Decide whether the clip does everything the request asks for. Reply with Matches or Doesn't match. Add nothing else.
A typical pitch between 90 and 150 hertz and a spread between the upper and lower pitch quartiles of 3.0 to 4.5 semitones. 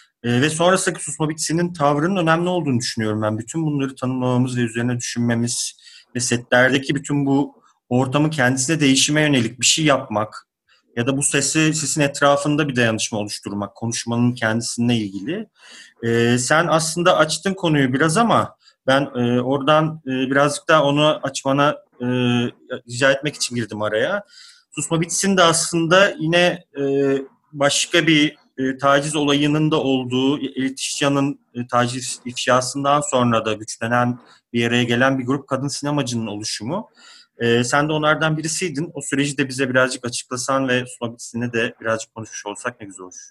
Matches